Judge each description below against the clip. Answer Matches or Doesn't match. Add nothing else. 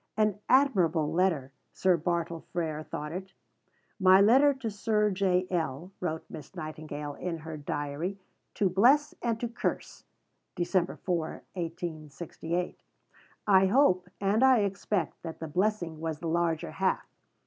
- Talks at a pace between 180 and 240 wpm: Doesn't match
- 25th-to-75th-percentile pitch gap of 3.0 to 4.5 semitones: Matches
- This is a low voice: Doesn't match